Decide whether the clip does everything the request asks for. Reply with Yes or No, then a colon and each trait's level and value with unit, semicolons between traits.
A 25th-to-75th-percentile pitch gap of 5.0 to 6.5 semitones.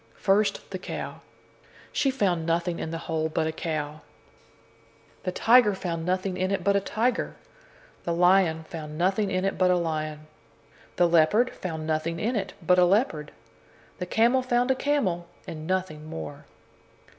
No: average, 3.8 semitones